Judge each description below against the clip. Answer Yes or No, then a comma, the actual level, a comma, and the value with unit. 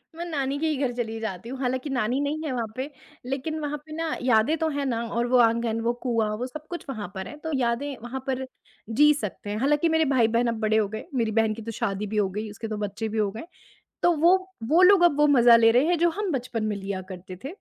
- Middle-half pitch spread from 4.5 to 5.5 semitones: Yes, average, 5.1 semitones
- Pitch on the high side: Yes, high, 245 Hz